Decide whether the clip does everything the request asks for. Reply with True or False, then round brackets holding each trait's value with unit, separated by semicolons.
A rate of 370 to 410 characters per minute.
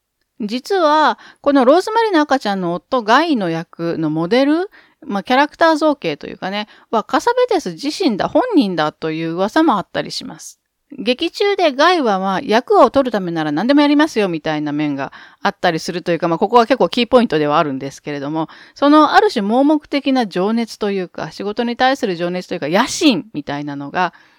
True (400 characters per minute)